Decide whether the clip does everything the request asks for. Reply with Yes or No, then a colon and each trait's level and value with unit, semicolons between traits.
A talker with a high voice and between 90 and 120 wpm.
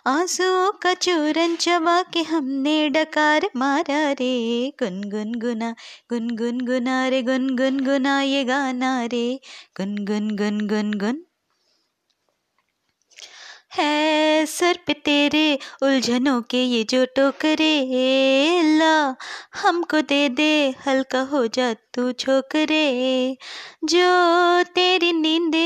Yes: very high, 275 Hz; slow, 110 wpm